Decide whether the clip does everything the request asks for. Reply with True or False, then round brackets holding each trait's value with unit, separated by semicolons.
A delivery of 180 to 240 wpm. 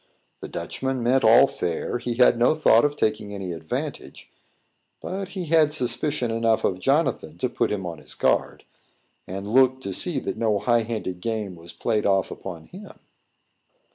False (170 wpm)